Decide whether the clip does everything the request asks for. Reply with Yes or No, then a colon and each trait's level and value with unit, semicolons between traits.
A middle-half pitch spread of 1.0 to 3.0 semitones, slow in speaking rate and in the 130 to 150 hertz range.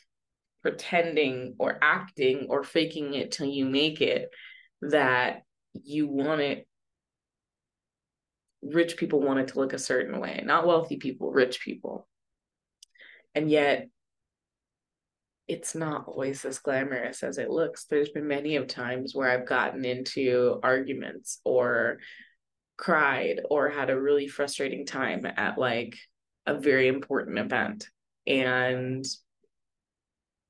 Yes: average, 2.7 semitones; slow, 125 wpm; medium, 140 Hz